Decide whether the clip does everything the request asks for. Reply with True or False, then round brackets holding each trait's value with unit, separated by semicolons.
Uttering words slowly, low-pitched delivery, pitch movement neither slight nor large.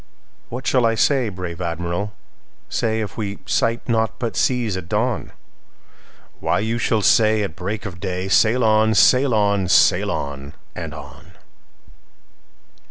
True (130 wpm; 110 Hz; 3.6 semitones)